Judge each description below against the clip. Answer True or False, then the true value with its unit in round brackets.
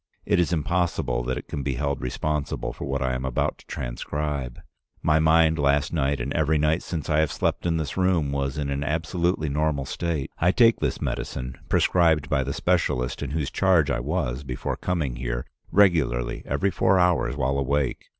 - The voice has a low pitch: True (75 Hz)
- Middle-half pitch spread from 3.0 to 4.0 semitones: True (3.4 semitones)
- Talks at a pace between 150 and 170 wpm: False (190 wpm)